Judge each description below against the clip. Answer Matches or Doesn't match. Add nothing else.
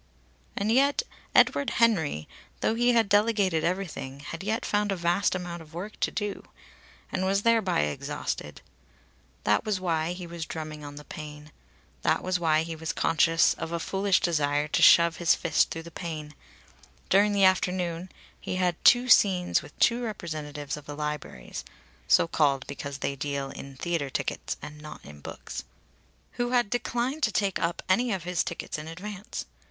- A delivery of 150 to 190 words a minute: Matches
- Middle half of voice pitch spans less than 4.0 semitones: Doesn't match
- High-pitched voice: Doesn't match